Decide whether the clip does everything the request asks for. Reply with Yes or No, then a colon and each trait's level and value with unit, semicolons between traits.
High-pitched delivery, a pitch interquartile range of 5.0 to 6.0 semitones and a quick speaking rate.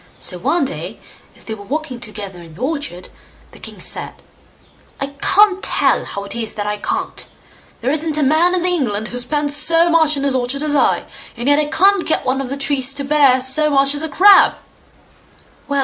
No: very high, 280 Hz; average, 4.0 semitones; fast, 210 wpm